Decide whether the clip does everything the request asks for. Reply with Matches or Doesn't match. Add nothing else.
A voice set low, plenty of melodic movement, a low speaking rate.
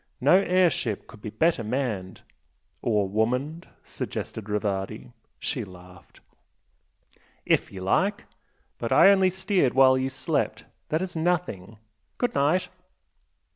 Matches